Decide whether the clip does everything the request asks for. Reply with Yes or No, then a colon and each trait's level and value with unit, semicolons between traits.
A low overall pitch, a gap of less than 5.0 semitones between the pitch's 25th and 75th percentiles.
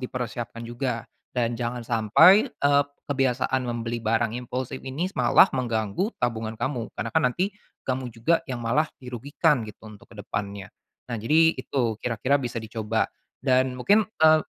Yes: low, 125 Hz; average, 2.9 semitones